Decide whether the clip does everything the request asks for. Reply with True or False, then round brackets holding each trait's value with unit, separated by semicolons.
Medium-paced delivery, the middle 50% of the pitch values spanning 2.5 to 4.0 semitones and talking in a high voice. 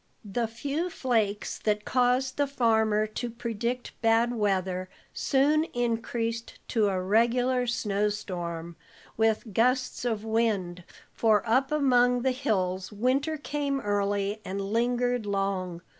False (125 wpm; 3.5 semitones; 225 Hz)